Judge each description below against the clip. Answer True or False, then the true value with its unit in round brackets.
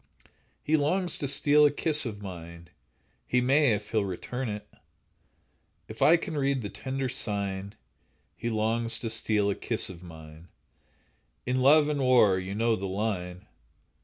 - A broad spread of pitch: True (5.8 semitones)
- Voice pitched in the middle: False (115 Hz)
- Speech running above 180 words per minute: False (155 wpm)